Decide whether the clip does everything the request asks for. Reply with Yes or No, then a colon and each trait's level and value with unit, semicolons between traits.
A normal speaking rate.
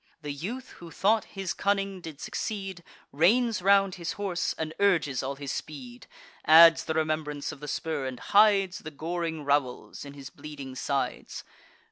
Yes: average, 160 wpm